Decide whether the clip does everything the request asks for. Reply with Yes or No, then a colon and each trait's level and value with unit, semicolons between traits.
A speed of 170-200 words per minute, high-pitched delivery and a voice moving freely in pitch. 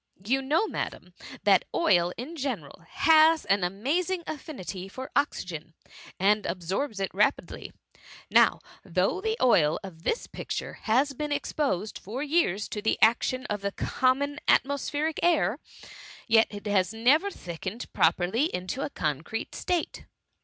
No: average, 145 wpm; high, 230 Hz; wide, 7.4 semitones